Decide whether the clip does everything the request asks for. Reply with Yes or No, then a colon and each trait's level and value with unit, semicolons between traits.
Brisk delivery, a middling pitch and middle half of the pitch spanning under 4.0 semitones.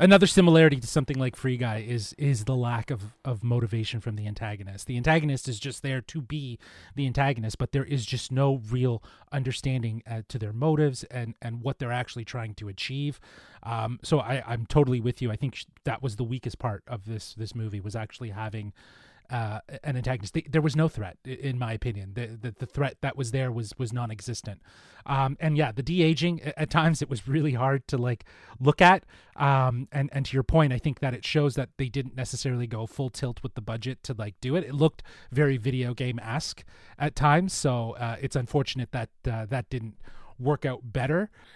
No: fast, 210 wpm; low, 130 Hz; average, 3.2 semitones